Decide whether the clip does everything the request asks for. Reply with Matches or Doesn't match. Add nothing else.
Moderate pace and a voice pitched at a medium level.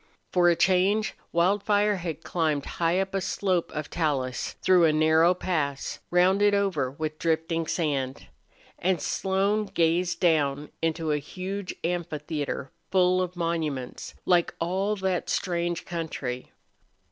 Doesn't match